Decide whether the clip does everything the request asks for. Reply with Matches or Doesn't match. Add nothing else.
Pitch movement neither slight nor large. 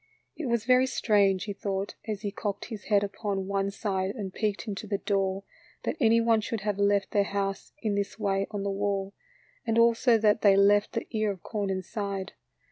Doesn't match